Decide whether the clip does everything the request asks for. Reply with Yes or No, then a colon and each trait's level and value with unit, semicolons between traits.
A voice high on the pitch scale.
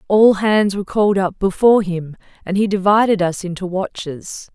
Yes: high, 195 Hz